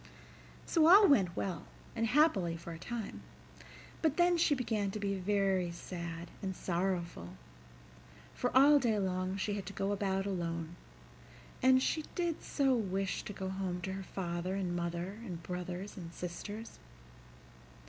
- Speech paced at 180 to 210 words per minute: No, average, 155 wpm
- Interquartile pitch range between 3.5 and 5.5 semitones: Yes, average, 4.1 semitones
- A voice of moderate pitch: No, high, 195 Hz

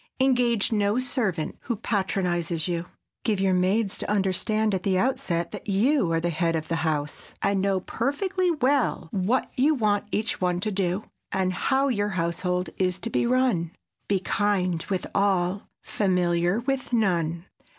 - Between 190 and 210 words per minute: No, average, 160 wpm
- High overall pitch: Yes, high, 195 Hz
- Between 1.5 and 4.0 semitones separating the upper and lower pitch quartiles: No, average, 4.5 semitones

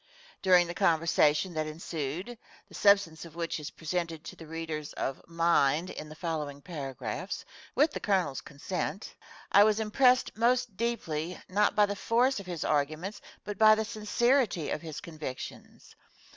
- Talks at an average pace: Yes, average, 160 wpm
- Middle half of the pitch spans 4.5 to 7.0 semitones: Yes, average, 5.1 semitones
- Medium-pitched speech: Yes, medium, 170 Hz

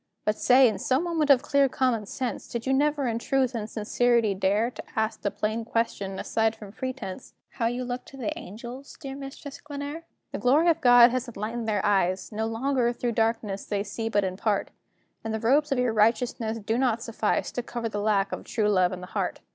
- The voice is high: Yes, high, 230 Hz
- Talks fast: Yes, fast, 215 wpm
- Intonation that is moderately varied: Yes, average, 3.4 semitones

